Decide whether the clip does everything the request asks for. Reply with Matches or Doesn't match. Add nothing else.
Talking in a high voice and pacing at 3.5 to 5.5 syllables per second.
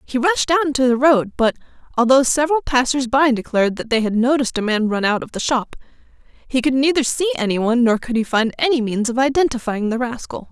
Doesn't match